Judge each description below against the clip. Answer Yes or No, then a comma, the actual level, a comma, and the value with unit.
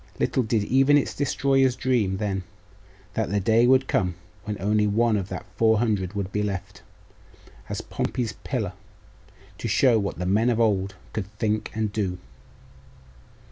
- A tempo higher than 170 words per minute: No, average, 160 wpm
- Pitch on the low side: Yes, low, 105 Hz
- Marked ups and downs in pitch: No, average, 3.3 semitones